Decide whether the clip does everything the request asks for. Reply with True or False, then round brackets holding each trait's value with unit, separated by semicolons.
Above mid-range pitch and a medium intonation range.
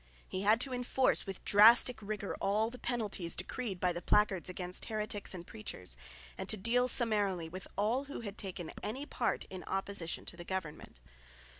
True (205 Hz; 3.8 semitones)